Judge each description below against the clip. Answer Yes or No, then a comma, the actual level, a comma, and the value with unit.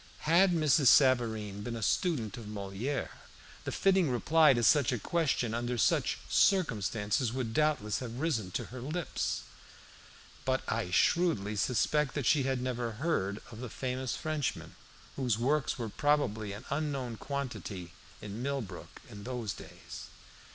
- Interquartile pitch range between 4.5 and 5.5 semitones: Yes, average, 5.1 semitones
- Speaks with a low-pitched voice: Yes, low, 125 Hz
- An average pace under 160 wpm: Yes, average, 145 wpm